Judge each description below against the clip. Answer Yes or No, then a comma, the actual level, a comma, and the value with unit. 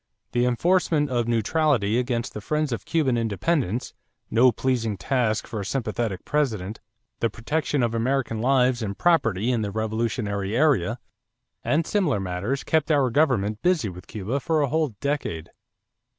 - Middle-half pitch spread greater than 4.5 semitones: Yes, average, 4.9 semitones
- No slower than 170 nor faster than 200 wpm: No, average, 150 wpm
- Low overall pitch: Yes, low, 120 Hz